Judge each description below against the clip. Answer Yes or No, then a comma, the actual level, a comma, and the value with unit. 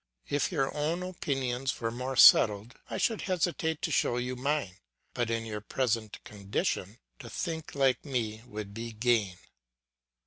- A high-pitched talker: No, low, 125 Hz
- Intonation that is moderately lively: Yes, average, 4.9 semitones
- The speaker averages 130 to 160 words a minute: Yes, average, 150 wpm